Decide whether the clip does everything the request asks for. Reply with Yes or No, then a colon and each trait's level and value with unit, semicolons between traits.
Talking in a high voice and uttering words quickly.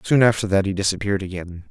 No: low, 100 Hz; fast, 210 wpm